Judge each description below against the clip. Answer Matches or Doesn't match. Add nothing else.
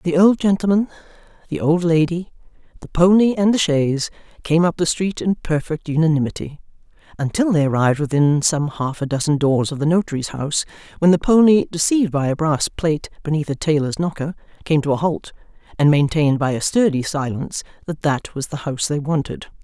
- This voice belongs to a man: Doesn't match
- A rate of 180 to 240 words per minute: Matches